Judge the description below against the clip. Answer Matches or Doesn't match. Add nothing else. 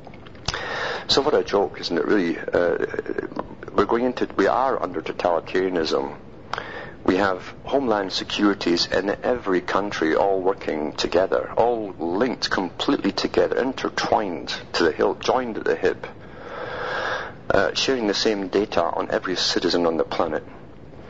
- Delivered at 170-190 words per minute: Doesn't match